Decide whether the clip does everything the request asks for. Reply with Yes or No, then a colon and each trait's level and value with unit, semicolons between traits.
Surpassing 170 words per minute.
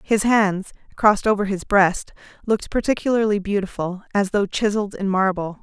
No: average, 150 wpm